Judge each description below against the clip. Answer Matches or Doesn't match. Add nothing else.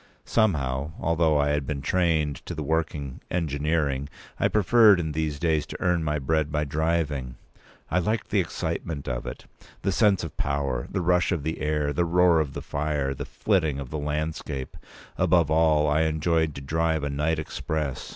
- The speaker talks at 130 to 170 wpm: Doesn't match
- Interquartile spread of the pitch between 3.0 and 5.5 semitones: Doesn't match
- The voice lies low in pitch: Matches